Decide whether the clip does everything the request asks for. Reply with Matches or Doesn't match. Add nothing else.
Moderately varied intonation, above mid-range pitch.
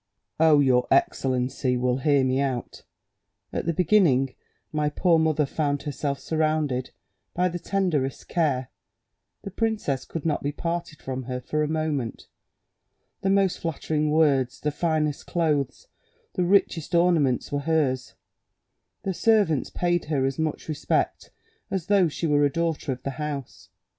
Doesn't match